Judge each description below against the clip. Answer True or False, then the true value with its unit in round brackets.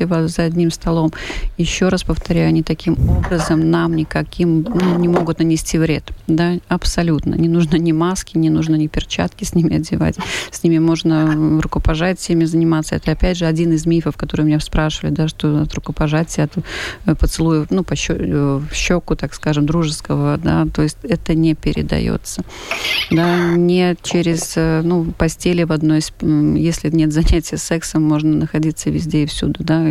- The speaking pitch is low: False (160 Hz)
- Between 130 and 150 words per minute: False (160 wpm)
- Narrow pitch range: True (1.5 semitones)